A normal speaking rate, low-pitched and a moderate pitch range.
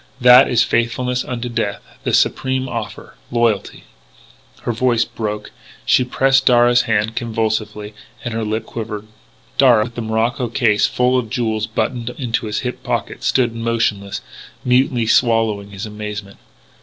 No: average, 145 wpm; low, 115 Hz; narrow, 2.3 semitones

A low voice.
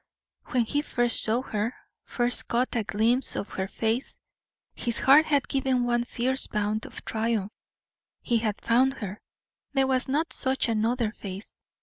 No: high, 240 Hz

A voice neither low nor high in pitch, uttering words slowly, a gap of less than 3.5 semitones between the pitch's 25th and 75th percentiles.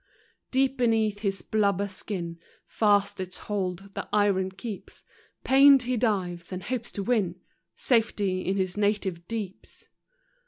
No: high, 205 Hz; slow, 130 wpm; average, 3.1 semitones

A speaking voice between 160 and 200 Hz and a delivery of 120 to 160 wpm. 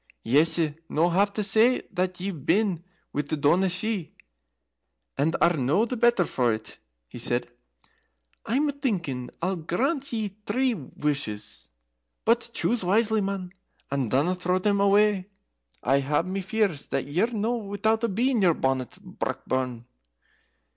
Yes: medium, 185 Hz; average, 145 wpm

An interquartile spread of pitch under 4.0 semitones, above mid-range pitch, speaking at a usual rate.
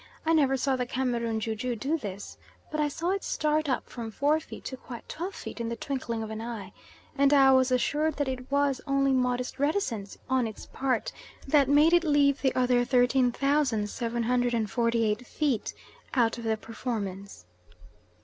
Yes: average, 3.5 semitones; very high, 255 Hz; average, 175 wpm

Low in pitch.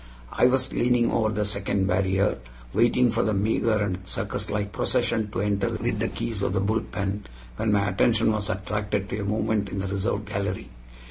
Yes: low, 105 Hz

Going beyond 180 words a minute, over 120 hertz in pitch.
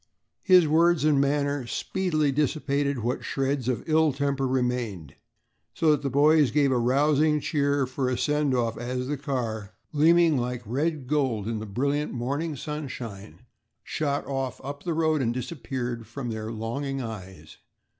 No: average, 155 wpm; medium, 140 Hz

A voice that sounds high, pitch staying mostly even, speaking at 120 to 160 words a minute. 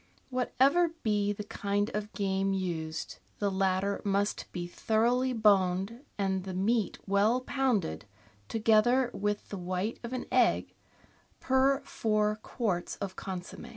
No: high, 205 Hz; average, 3.6 semitones; slow, 135 wpm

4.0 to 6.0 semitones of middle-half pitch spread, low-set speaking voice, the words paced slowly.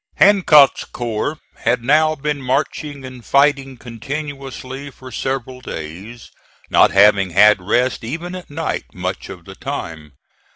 Yes: average, 5.2 semitones; low, 130 Hz; slow, 130 wpm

